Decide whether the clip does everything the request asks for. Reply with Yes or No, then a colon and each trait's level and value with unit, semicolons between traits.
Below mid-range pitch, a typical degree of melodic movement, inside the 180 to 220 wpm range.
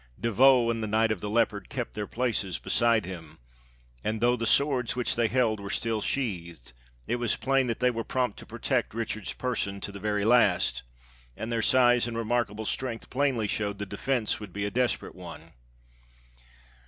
Yes: low, 115 Hz; average, 3.0 semitones; average, 190 wpm